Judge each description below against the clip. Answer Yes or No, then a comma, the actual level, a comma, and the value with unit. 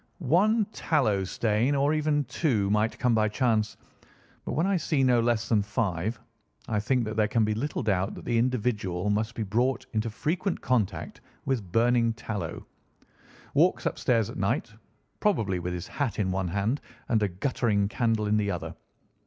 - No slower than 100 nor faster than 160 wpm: No, average, 170 wpm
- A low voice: Yes, low, 110 Hz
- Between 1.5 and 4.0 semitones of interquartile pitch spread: Yes, average, 3.6 semitones